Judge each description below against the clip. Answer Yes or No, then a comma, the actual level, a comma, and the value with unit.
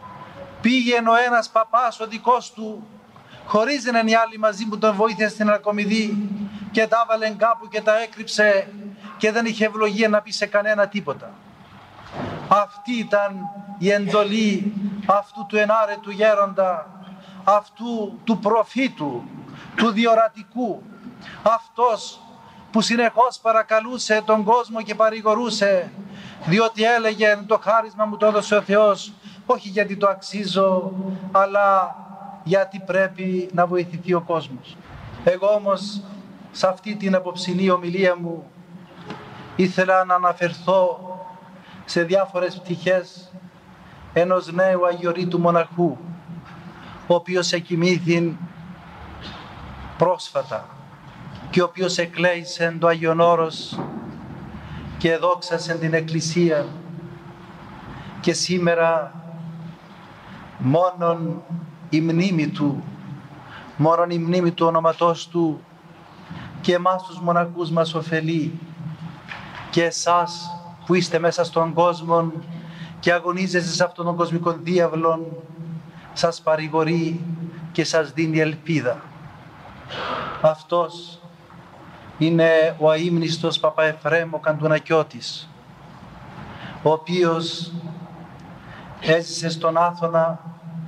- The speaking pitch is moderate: Yes, medium, 180 Hz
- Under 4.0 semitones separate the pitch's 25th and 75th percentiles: Yes, average, 3.6 semitones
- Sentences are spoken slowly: Yes, slow, 100 wpm